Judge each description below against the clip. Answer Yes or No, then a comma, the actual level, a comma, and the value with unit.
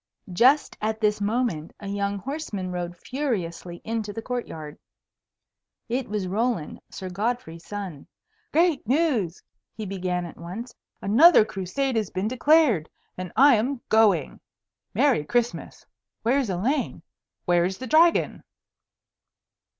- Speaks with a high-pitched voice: Yes, high, 215 Hz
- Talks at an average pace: No, slow, 125 wpm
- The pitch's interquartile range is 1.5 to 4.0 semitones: No, wide, 5.6 semitones